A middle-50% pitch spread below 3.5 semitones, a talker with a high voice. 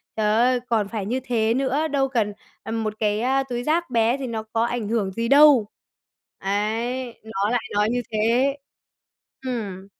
Yes: average, 3.0 semitones; high, 230 Hz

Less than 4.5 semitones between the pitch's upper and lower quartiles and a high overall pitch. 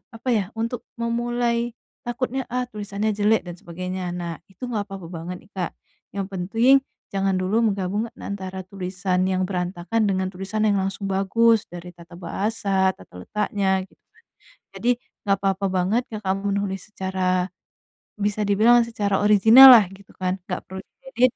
Yes: average, 3.0 semitones; high, 195 Hz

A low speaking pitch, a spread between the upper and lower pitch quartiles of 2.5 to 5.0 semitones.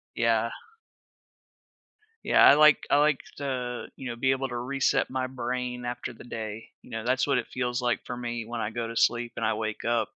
No: low, 120 Hz; narrow, 2.0 semitones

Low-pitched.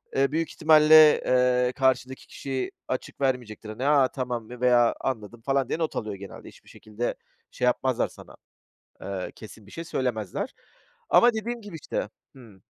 Yes: low, 130 Hz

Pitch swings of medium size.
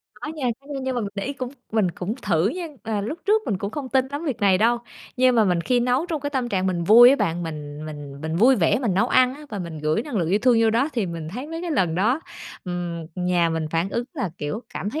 No: wide, 7.0 semitones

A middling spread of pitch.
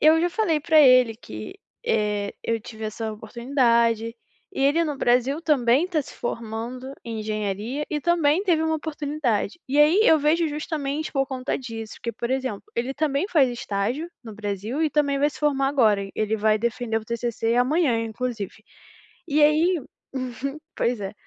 Yes: average, 5.0 semitones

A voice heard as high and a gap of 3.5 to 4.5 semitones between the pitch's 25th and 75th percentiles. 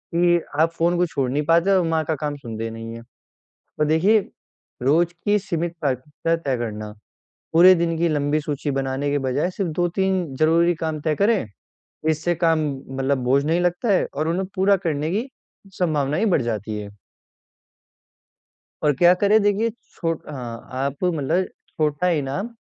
No: medium, 160 Hz; average, 4.2 semitones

